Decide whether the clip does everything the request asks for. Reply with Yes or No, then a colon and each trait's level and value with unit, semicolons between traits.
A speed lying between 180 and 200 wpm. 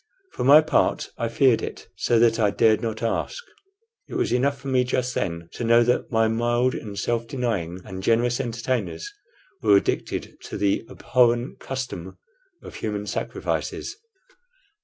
No: average, 160 wpm